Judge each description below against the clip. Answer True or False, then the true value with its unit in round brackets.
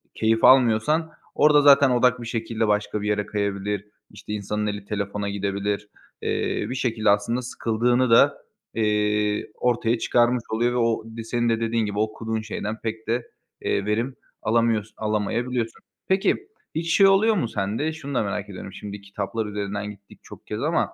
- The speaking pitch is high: False (110 Hz)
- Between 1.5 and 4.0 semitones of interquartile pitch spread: True (2.7 semitones)